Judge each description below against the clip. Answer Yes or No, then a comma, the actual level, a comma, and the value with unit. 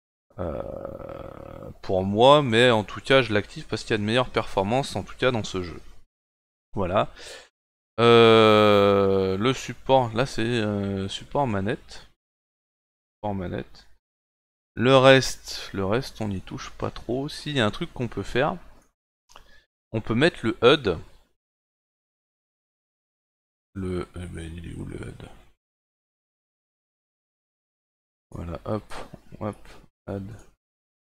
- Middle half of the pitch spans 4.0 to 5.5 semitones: Yes, average, 4.3 semitones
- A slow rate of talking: Yes, slow, 125 wpm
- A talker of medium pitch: No, low, 105 Hz